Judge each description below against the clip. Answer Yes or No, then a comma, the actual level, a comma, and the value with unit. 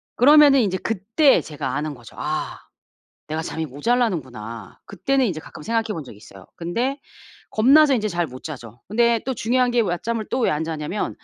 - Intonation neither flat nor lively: No, wide, 8.2 semitones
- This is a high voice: Yes, high, 200 Hz